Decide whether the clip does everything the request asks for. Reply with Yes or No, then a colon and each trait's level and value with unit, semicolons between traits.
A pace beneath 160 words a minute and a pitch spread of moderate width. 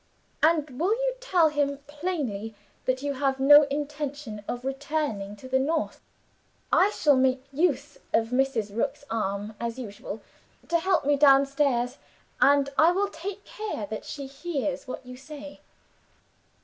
Yes: average, 150 wpm; average, 3.2 semitones